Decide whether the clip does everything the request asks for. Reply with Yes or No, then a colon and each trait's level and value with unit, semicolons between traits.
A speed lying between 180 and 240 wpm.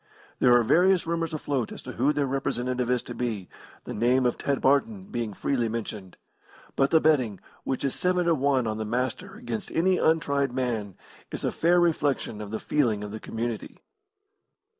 Yes: average, 185 wpm